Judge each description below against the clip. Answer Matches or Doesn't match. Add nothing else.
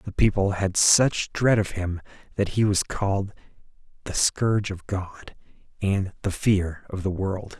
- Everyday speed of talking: Matches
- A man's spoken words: Matches